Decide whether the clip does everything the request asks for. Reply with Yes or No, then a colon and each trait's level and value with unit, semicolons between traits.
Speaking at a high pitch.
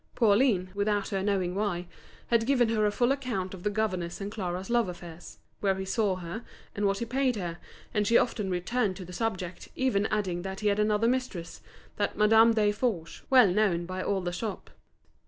Yes: high, 205 Hz